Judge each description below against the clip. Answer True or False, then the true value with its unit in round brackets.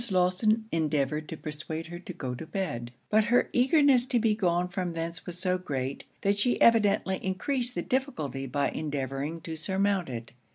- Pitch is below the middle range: False (180 Hz)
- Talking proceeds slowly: False (175 wpm)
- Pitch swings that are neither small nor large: False (5.7 semitones)